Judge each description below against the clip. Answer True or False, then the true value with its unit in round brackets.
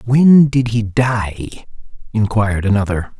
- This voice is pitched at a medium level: False (110 Hz)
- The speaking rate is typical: False (115 wpm)